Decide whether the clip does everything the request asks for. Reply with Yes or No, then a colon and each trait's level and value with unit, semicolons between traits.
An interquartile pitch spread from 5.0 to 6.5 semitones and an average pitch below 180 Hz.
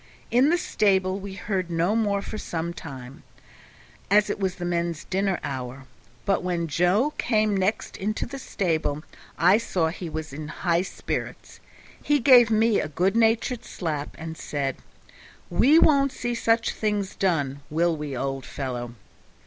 No: average, 5.3 semitones; medium, 185 Hz